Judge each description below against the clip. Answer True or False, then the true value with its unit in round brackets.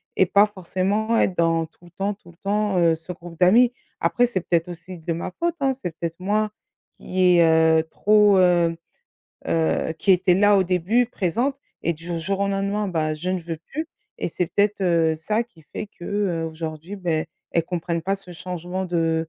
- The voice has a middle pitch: True (180 Hz)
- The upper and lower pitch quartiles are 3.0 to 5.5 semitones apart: True (3.5 semitones)